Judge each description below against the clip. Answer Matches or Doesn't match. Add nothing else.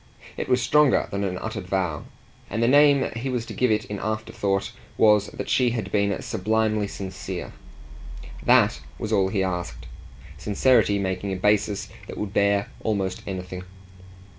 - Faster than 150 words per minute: Matches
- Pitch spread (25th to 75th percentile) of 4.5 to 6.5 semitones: Doesn't match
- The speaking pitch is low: Matches